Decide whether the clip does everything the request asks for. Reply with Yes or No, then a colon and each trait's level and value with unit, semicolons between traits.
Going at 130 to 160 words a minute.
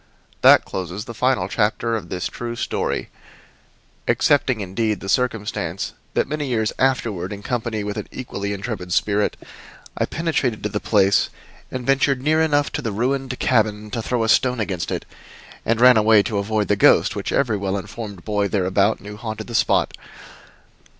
No: average, 170 wpm